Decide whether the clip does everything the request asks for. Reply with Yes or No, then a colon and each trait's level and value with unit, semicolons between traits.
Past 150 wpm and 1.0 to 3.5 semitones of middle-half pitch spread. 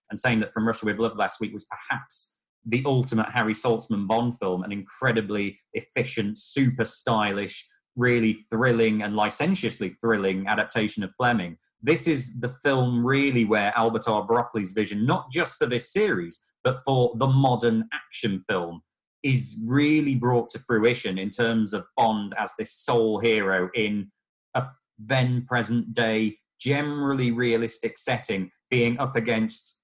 No: average, 145 wpm; average, 2.9 semitones